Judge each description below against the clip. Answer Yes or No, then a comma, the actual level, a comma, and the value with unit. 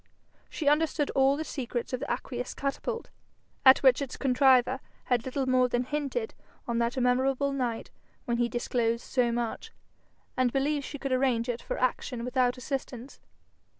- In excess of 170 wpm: No, average, 160 wpm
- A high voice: Yes, very high, 255 Hz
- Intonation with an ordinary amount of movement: No, narrow, 2.2 semitones